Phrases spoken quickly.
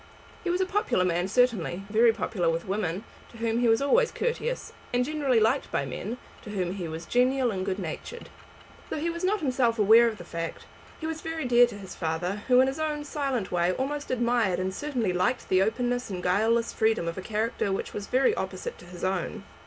Yes: fast, 215 wpm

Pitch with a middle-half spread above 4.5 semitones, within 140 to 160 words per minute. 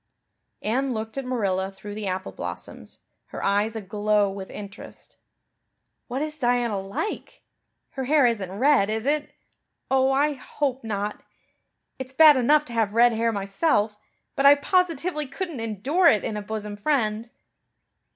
Yes: average, 5.1 semitones; average, 150 wpm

